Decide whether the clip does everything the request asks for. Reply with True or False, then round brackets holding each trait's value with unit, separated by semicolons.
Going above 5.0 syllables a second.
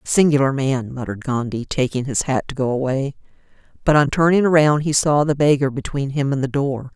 True (5.5 syllables/s)